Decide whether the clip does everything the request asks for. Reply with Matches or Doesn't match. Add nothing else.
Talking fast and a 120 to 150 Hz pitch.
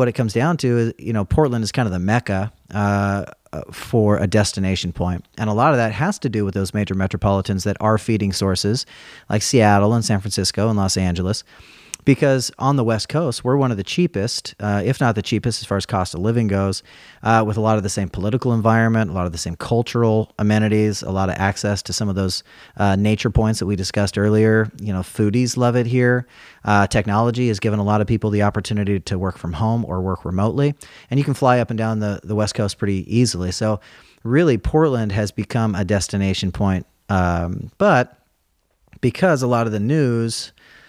Doesn't match